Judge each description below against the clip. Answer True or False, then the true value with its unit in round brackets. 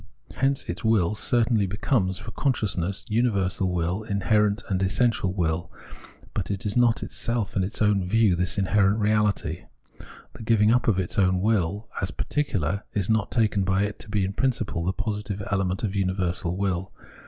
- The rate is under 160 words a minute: False (165 wpm)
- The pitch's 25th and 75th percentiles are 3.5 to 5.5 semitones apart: False (2.9 semitones)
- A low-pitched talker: True (100 Hz)